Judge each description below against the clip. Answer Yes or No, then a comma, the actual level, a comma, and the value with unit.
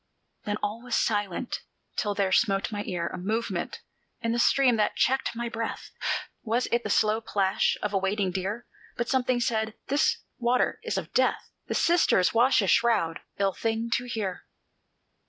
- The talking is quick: No, average, 175 wpm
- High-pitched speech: Yes, high, 220 Hz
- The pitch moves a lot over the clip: No, average, 3.2 semitones